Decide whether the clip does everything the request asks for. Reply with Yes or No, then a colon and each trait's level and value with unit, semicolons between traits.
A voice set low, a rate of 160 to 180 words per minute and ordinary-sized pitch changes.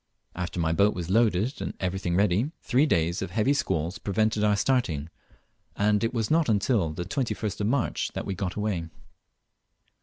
Yes: low, 100 Hz; average, 175 wpm; average, 4.5 semitones